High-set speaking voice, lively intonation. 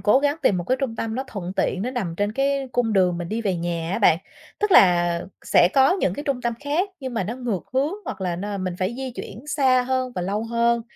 Yes: high, 230 Hz; wide, 5.9 semitones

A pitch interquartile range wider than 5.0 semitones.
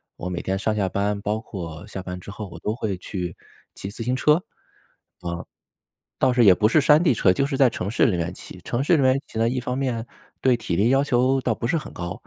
Yes: wide, 5.4 semitones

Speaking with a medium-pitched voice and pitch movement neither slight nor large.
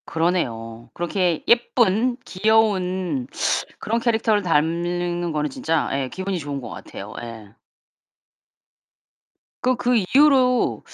No: medium, 180 Hz; wide, 6.3 semitones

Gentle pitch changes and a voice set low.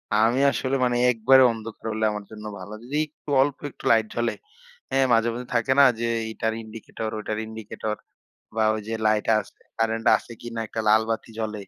Yes: narrow, 1.6 semitones; low, 110 Hz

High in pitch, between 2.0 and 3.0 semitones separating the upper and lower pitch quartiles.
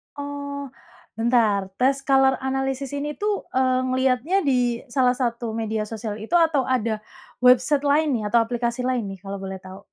No: very high, 255 Hz; average, 3.4 semitones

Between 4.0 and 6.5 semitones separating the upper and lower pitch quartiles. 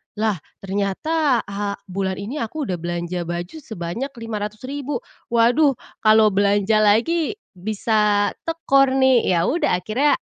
Yes: average, 5.1 semitones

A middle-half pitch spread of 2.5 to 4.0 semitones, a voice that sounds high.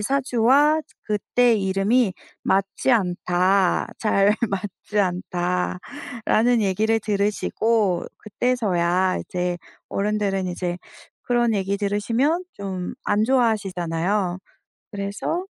Yes: average, 3.7 semitones; high, 200 Hz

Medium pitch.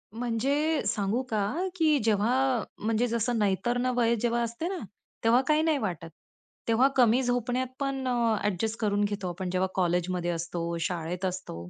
No: high, 225 Hz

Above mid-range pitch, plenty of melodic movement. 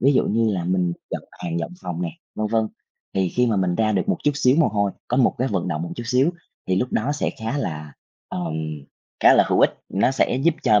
No: low, 105 Hz; wide, 5.8 semitones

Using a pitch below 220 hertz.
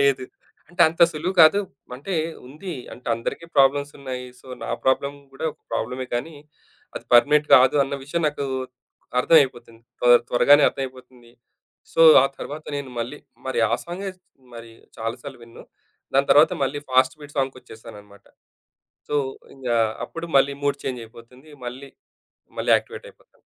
Yes: low, 135 Hz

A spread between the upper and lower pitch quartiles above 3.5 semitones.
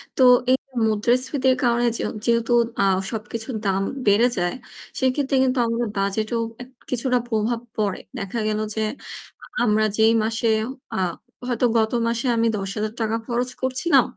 No: narrow, 2.6 semitones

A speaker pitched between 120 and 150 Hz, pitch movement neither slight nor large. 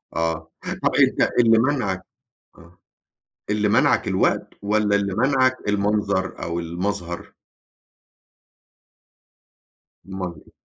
No: low, 100 Hz; average, 3.5 semitones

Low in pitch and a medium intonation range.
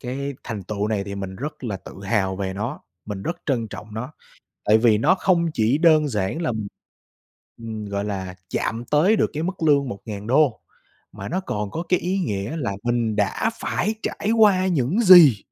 No: low, 120 Hz; wide, 7.5 semitones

